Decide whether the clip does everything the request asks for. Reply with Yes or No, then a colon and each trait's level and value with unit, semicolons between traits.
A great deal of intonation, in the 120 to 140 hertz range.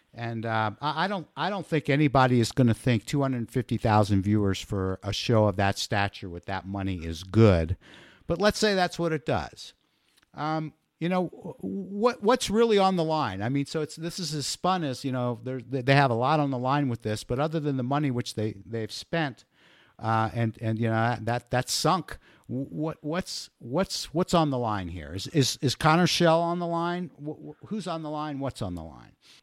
Yes: wide, 6.4 semitones; low, 135 Hz